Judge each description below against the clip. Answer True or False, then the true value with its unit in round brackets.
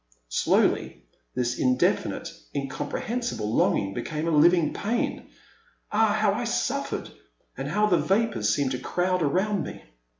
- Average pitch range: False (8.1 semitones)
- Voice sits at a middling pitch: True (175 Hz)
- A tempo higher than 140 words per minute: False (135 wpm)